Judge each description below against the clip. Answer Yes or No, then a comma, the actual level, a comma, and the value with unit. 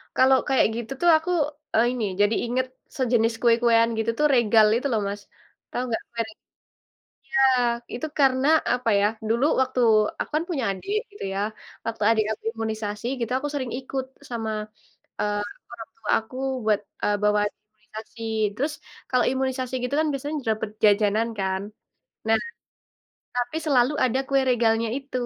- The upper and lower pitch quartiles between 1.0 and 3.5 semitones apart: Yes, average, 3.2 semitones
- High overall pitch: Yes, high, 235 Hz